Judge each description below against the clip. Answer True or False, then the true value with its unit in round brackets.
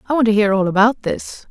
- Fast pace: True (280 wpm)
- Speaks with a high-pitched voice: True (220 Hz)